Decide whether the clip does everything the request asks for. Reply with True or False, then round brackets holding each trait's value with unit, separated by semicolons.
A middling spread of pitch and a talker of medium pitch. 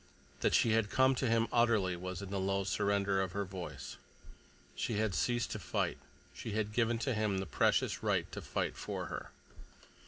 False (3.0 semitones; 105 Hz)